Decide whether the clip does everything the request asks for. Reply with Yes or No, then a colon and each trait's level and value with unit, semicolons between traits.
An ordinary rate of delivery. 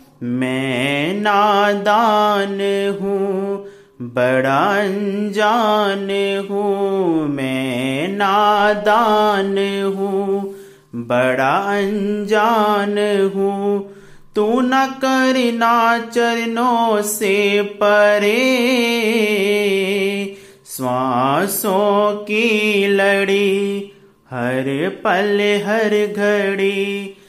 No: slow, 55 wpm